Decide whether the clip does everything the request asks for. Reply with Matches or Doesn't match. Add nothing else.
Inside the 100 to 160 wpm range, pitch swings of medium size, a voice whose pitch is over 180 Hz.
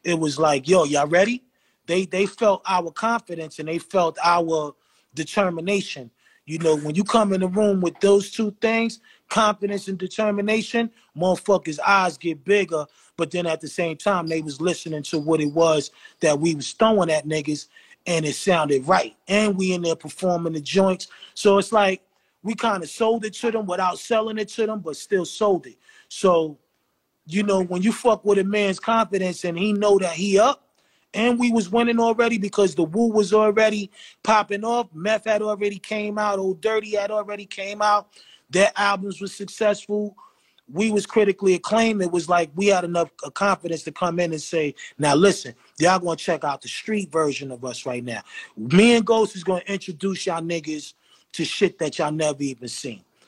Doesn't match